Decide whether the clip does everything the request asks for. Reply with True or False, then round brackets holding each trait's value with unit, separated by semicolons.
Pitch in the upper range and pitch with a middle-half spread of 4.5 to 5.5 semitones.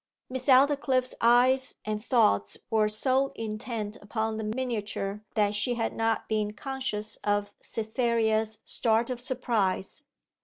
False (225 Hz; 3.1 semitones)